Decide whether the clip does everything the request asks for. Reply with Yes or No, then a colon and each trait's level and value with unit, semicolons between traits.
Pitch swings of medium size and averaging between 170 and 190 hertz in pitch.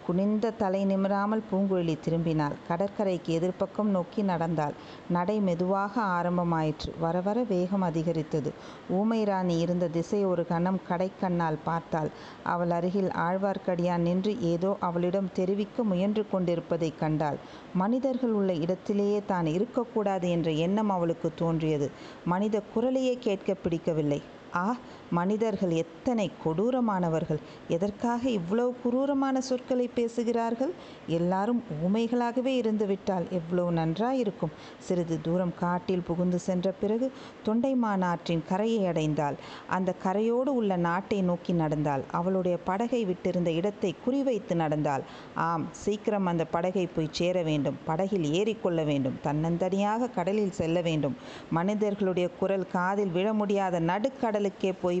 Yes: average, 3.7 semitones; medium, 185 Hz